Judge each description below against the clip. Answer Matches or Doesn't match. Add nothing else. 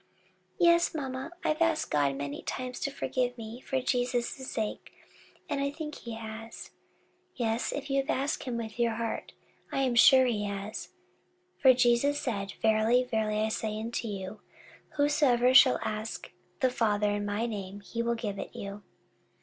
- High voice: Matches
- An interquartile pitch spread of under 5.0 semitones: Matches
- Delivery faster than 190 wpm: Doesn't match